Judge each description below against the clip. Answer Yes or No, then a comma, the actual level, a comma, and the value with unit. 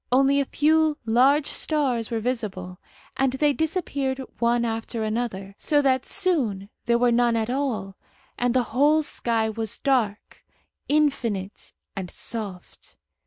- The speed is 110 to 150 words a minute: Yes, slow, 135 wpm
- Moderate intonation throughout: Yes, average, 4.1 semitones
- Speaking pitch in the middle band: No, high, 240 Hz